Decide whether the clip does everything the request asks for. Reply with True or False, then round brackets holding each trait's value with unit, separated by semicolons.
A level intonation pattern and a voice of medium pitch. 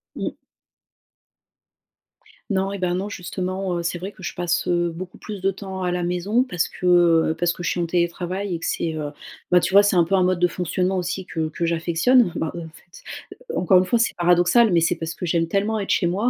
True (1.9 semitones; 180 Hz)